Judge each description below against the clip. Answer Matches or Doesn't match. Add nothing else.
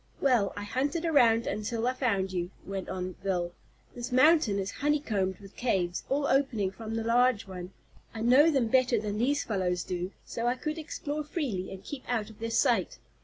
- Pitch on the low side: Doesn't match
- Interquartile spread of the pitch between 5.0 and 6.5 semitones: Matches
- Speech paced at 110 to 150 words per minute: Doesn't match